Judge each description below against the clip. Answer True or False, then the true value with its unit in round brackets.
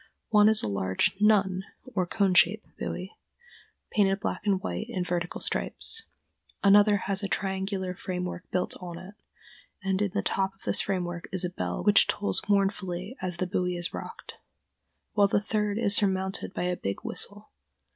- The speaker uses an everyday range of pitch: False (2.2 semitones)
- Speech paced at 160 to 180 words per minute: True (170 wpm)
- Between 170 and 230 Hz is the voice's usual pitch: True (190 Hz)